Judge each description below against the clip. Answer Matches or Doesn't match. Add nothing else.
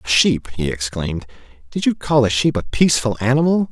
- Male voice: Matches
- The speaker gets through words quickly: Doesn't match